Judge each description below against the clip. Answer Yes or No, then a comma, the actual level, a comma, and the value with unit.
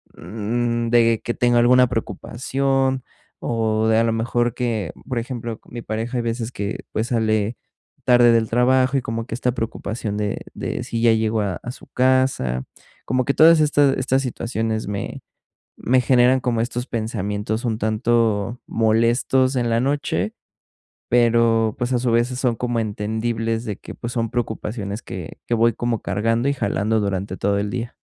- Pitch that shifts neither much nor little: No, narrow, 2.0 semitones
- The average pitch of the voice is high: No, low, 115 Hz